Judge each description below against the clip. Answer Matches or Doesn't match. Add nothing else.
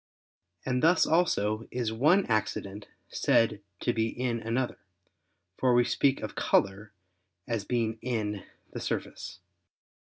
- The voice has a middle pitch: Doesn't match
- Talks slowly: Matches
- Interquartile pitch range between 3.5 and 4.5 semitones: Doesn't match